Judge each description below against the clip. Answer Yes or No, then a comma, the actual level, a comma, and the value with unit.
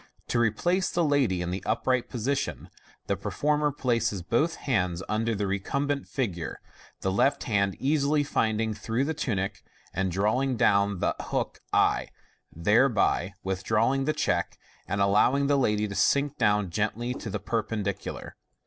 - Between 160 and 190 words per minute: No, average, 150 wpm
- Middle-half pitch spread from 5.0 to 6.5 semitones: Yes, wide, 5.6 semitones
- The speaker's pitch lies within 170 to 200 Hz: No, low, 110 Hz